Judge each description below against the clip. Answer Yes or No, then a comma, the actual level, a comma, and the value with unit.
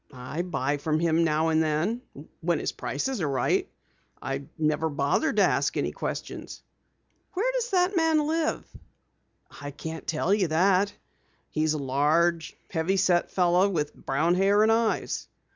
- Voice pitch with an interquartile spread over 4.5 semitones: Yes, average, 4.9 semitones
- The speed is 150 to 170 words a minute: Yes, average, 155 wpm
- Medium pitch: Yes, medium, 170 Hz